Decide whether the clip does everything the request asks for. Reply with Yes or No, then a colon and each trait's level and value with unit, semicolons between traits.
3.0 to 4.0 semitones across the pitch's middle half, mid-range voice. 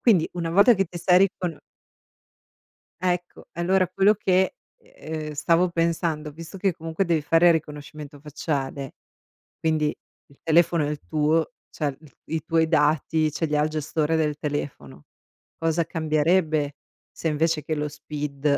No: narrow, 2.4 semitones; medium, 160 Hz